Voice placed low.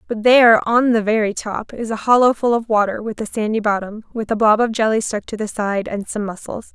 No: high, 220 Hz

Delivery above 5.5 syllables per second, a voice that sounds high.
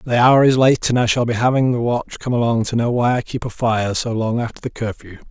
No: 5.8 syllables/s; low, 120 Hz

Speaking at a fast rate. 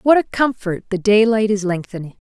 Yes: fast, 210 wpm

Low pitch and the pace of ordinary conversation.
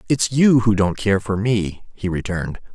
Yes: low, 105 Hz; average, 195 wpm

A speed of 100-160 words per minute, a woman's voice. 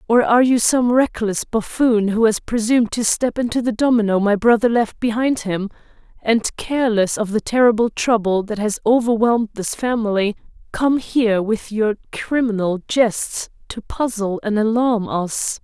Yes: average, 155 wpm; female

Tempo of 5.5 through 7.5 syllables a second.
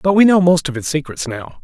Yes: 5.7 syllables/s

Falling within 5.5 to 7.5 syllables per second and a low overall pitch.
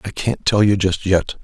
No: 4.6 syllables/s; low, 100 Hz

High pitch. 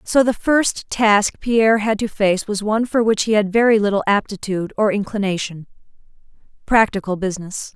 Yes: high, 210 Hz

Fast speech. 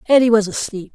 No: average, 190 wpm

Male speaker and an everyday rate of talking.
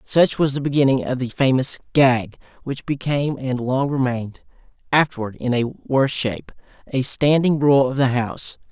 Yes: male; average, 150 wpm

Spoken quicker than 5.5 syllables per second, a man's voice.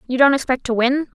No: 6.5 syllables/s; female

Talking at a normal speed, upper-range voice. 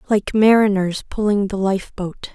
Yes: average, 155 wpm; high, 200 Hz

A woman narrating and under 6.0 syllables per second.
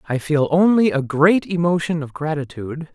No: male; 5.1 syllables/s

